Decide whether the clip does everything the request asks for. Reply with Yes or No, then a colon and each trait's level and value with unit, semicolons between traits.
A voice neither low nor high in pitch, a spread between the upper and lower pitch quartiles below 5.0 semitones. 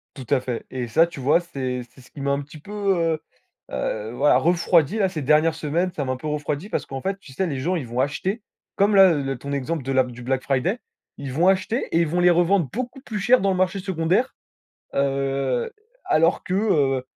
No: medium, 155 Hz; wide, 5.6 semitones